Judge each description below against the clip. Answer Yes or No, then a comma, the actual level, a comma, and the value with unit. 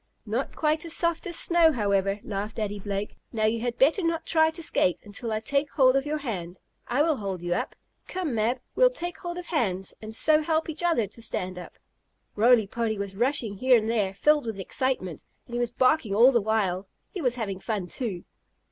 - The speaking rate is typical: No, fast, 215 wpm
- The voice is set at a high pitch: Yes, high, 235 Hz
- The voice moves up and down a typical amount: No, wide, 7.0 semitones